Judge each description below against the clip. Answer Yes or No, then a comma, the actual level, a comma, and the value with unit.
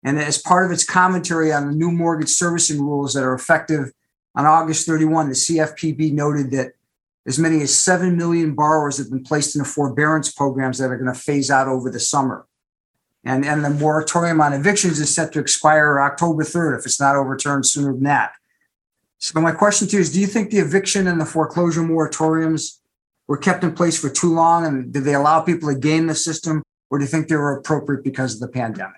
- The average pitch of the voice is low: No, medium, 155 Hz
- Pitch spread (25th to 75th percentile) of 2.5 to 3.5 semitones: Yes, average, 2.8 semitones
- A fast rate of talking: Yes, fast, 215 wpm